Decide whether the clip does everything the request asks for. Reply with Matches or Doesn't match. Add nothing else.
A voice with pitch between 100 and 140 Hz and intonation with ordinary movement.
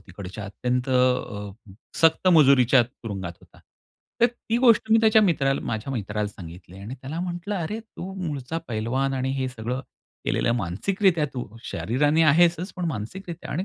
Doesn't match